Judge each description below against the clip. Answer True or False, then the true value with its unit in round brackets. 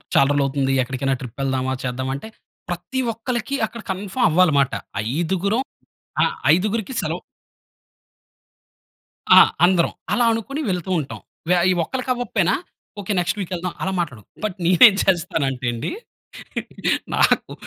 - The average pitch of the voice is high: False (175 Hz)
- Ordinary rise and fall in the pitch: False (7.7 semitones)